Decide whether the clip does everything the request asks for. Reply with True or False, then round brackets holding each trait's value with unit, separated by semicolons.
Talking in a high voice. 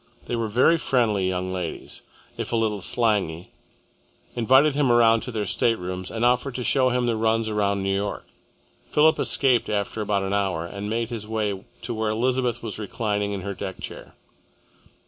False (110 Hz)